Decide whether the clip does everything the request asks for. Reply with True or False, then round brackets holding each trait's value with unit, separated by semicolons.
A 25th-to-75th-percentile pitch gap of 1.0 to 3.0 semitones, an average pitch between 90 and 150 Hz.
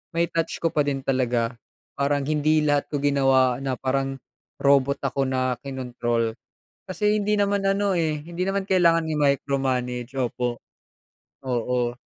False (4.2 semitones; 140 Hz)